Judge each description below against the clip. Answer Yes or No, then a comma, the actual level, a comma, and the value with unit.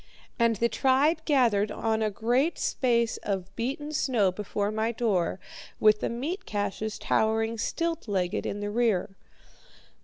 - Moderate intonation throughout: Yes, average, 3.6 semitones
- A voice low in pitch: No, high, 225 Hz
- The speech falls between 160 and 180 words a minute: No, average, 145 wpm